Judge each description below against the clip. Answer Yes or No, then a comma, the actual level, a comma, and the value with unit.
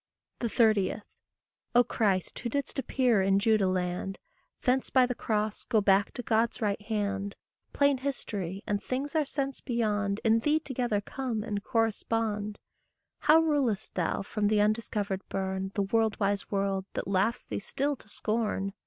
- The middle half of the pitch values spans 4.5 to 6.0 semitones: No, average, 3.5 semitones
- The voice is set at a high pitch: Yes, high, 215 Hz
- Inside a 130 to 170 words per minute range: Yes, average, 155 wpm